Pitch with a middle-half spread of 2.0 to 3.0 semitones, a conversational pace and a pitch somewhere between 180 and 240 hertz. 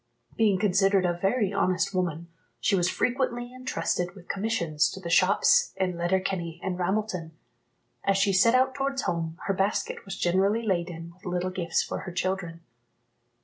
Yes: narrow, 2.6 semitones; average, 160 wpm; high, 190 Hz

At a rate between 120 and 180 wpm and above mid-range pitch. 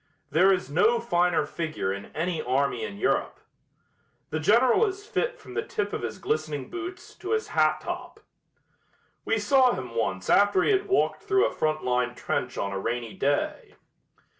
No: average, 175 wpm; medium, 175 Hz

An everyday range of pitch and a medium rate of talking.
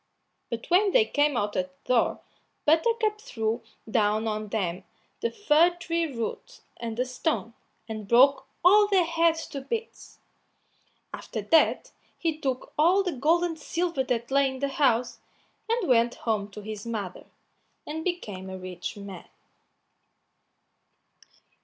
No: wide, 7.5 semitones; average, 145 wpm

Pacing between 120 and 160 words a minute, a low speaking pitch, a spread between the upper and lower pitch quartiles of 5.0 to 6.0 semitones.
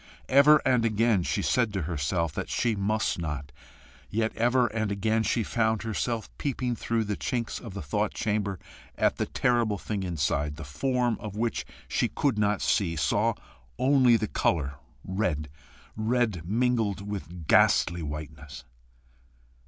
Yes: average, 150 wpm; low, 105 Hz; average, 5.3 semitones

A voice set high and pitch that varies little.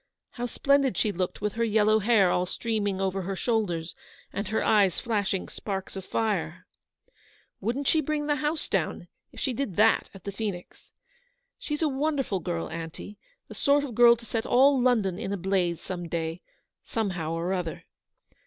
No: high, 205 Hz; average, 4.7 semitones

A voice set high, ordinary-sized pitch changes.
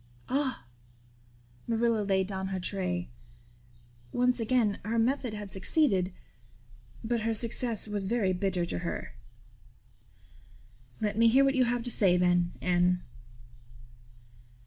Yes: high, 210 Hz; average, 4.1 semitones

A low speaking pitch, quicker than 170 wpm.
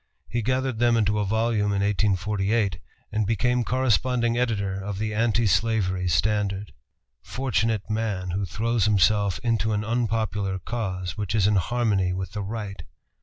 No: low, 105 Hz; average, 150 wpm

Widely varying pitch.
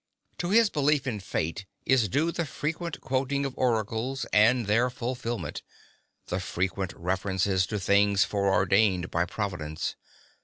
Yes: wide, 5.7 semitones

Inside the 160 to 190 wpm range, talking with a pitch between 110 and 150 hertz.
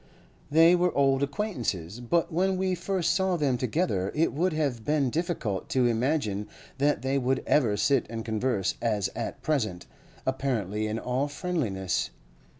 No: average, 150 wpm; low, 135 Hz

